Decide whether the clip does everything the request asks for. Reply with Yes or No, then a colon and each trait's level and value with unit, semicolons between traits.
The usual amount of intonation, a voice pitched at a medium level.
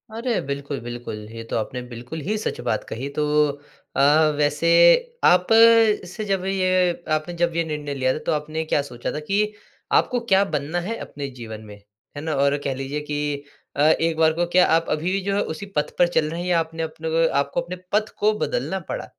Yes: average, 4.6 semitones; medium, 160 Hz